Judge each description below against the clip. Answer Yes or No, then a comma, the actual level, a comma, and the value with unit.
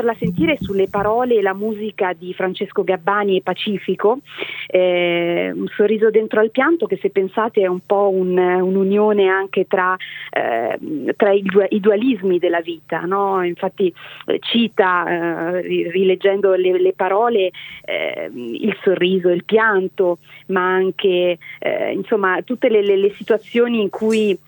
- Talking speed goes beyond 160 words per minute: No, average, 150 wpm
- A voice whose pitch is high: Yes, high, 195 Hz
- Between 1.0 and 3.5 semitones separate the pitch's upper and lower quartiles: Yes, average, 2.9 semitones